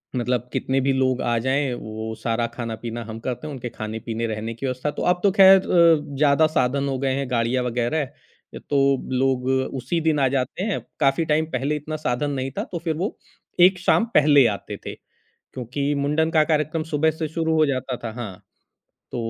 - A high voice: No, low, 135 Hz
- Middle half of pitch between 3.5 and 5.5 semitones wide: Yes, average, 4.0 semitones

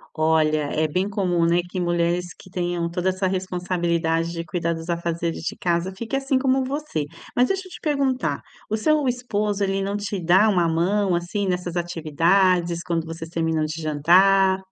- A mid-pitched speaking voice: Yes, medium, 180 Hz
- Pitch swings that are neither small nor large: Yes, average, 3.0 semitones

